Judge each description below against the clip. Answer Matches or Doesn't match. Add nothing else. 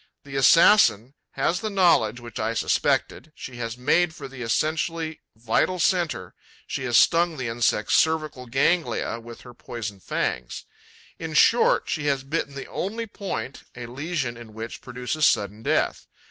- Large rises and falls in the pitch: Matches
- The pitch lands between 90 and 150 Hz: Matches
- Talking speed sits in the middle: Matches